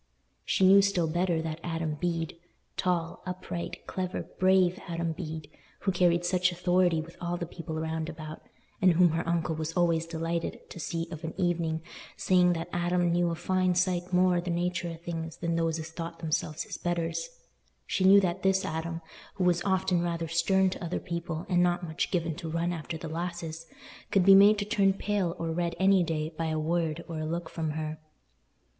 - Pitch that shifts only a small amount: Yes, narrow, 1.8 semitones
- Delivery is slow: No, average, 190 wpm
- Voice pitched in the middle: Yes, medium, 170 Hz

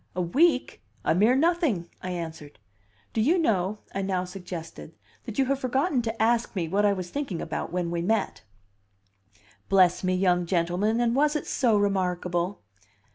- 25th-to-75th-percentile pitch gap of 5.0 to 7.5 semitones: Yes, average, 5.3 semitones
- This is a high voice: Yes, high, 195 Hz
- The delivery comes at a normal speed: Yes, average, 170 wpm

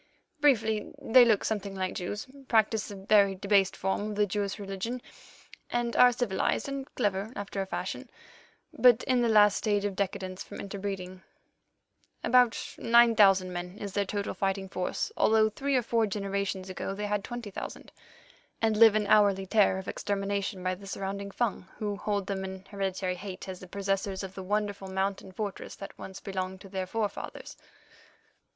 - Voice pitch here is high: Yes, high, 200 Hz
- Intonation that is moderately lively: No, narrow, 2.0 semitones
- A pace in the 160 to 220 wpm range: Yes, average, 165 wpm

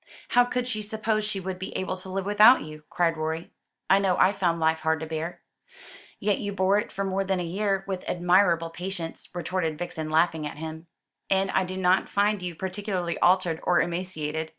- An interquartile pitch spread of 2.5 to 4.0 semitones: Yes, average, 3.0 semitones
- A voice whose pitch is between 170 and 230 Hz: Yes, medium, 185 Hz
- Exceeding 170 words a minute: Yes, average, 200 wpm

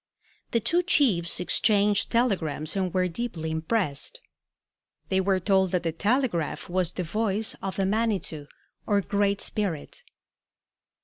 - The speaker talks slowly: Yes, slow, 130 wpm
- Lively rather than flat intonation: No, average, 4.1 semitones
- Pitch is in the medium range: No, high, 195 Hz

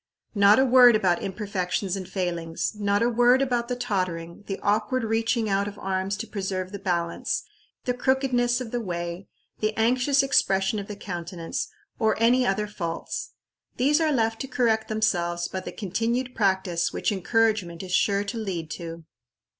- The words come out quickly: No, average, 170 wpm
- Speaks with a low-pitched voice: No, high, 205 Hz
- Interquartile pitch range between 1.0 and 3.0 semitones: No, average, 4.2 semitones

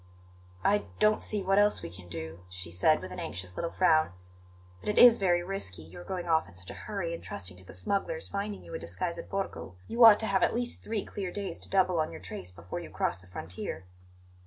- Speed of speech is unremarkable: No, fast, 235 wpm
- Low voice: No, medium, 170 Hz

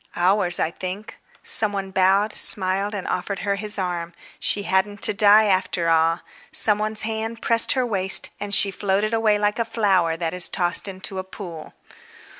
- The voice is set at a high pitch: Yes, high, 195 Hz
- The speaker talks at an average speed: Yes, average, 180 wpm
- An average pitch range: No, narrow, 2.3 semitones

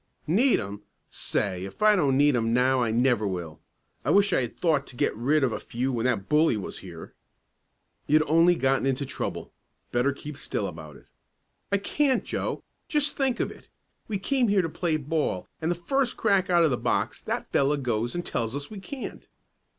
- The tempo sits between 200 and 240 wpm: Yes, fast, 205 wpm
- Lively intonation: Yes, wide, 6.9 semitones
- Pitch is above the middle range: No, medium, 140 Hz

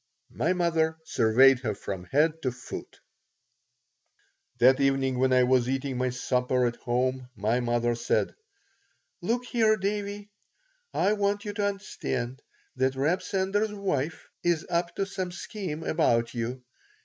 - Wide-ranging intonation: Yes, wide, 7.4 semitones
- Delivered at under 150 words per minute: Yes, average, 140 wpm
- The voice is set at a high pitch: No, low, 135 Hz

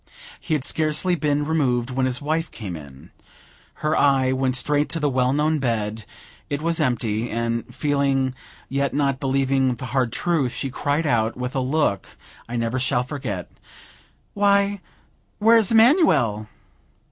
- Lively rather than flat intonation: No, average, 3.9 semitones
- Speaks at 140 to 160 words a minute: Yes, average, 150 wpm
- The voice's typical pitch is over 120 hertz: Yes, low, 135 Hz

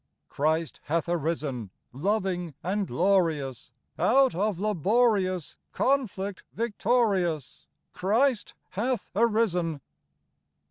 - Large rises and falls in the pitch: No, average, 4.9 semitones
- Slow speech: Yes, slow, 80 wpm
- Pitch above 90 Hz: Yes, high, 190 Hz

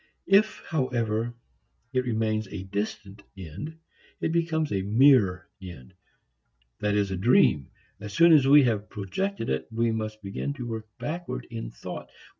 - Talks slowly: No, average, 150 wpm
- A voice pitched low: Yes, low, 110 Hz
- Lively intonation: Yes, wide, 5.7 semitones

